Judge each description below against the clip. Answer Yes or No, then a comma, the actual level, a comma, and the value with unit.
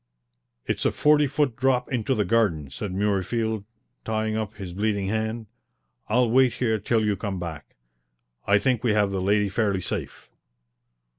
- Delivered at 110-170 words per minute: Yes, average, 160 wpm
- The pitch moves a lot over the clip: No, average, 2.9 semitones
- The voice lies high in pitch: No, low, 110 Hz